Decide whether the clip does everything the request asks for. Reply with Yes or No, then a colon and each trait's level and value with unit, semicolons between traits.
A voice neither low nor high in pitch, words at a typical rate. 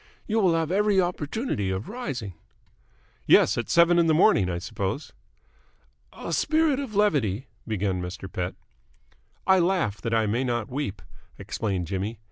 No: low, 125 Hz; average, 155 wpm